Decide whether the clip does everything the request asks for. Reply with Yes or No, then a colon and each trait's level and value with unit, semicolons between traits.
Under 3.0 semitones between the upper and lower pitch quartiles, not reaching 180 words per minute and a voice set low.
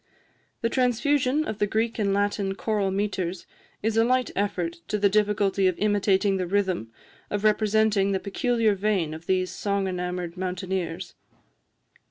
No: narrow, 2.4 semitones; average, 150 wpm; high, 200 Hz